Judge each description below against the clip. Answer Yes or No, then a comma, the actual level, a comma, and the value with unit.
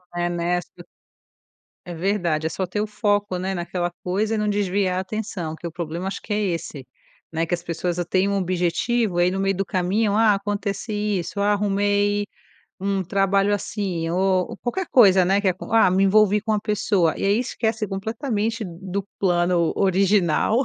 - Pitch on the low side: No, high, 195 Hz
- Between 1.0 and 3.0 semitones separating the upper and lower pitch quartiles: Yes, average, 2.7 semitones